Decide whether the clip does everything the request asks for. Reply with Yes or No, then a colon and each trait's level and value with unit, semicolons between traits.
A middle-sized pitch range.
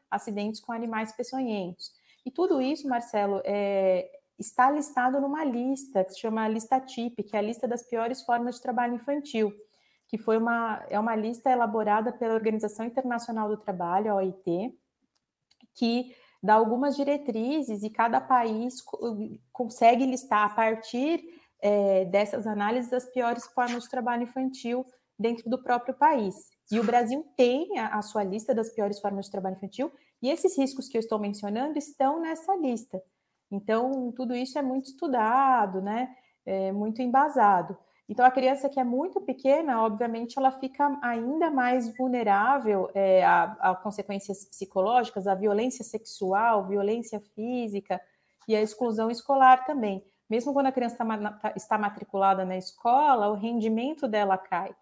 Yes: average, 3.8 semitones